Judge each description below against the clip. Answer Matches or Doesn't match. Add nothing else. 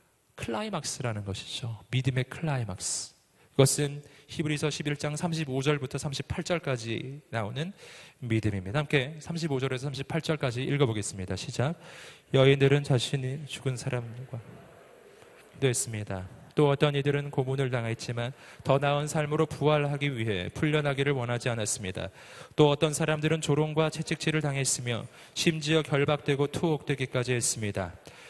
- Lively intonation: Doesn't match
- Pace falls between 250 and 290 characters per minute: Doesn't match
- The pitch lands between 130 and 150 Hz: Matches